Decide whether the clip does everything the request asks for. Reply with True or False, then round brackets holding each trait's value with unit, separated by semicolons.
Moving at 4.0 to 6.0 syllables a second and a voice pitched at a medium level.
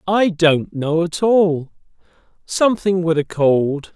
False (3.6 syllables/s; 170 Hz)